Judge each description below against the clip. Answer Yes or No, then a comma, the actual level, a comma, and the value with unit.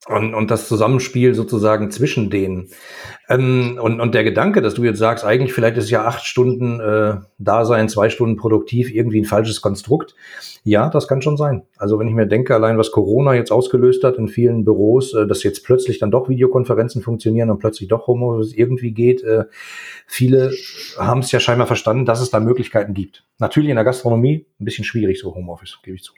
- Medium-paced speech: No, fast, 200 wpm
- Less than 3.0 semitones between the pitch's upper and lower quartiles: Yes, narrow, 2.6 semitones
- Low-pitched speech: Yes, low, 115 Hz